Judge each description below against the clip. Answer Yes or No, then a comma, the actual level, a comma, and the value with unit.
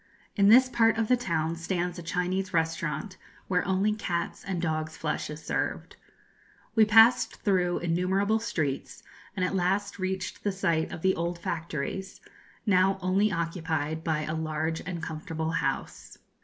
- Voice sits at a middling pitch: Yes, medium, 180 Hz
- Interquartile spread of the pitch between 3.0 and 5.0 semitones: Yes, average, 3.4 semitones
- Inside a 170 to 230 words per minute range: No, average, 155 wpm